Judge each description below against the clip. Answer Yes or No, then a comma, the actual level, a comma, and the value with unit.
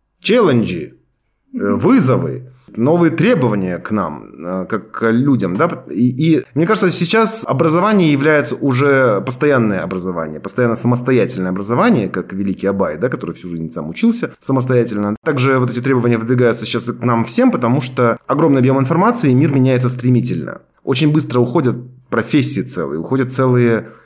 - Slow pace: No, average, 145 wpm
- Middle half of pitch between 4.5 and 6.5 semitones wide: No, average, 3.8 semitones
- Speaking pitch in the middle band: No, low, 125 Hz